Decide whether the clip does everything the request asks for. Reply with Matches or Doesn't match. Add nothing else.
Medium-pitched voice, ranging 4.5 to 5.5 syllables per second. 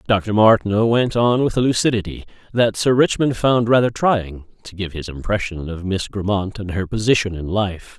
Doesn't match